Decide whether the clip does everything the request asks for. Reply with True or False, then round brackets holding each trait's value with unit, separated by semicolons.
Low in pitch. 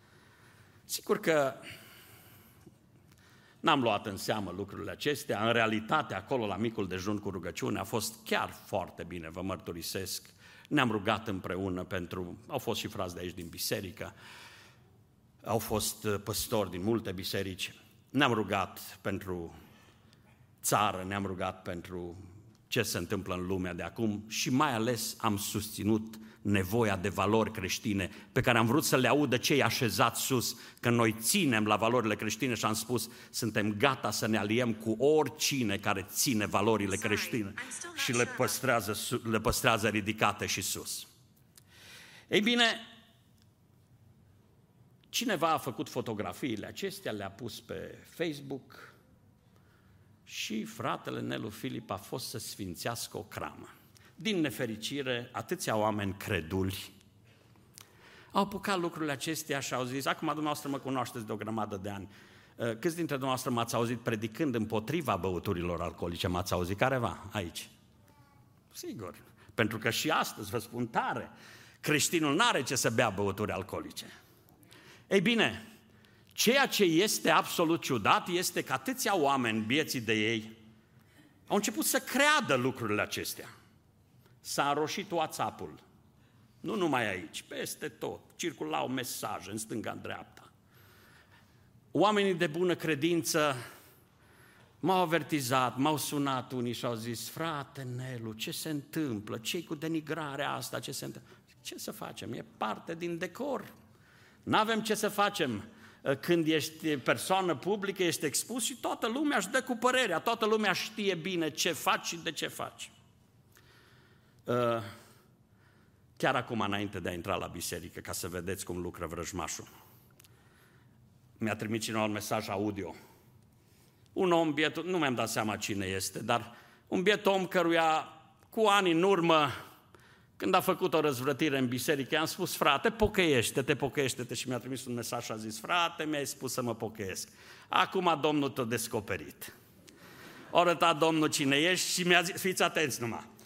True (120 Hz)